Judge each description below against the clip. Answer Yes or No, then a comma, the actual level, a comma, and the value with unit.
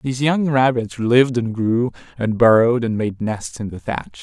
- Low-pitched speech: Yes, low, 120 Hz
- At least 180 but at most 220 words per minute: Yes, average, 200 wpm